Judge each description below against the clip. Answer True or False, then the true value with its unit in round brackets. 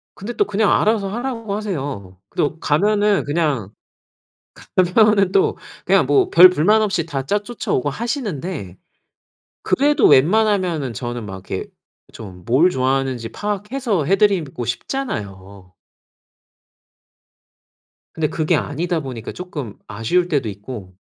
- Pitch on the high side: False (165 Hz)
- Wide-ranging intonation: True (8.9 semitones)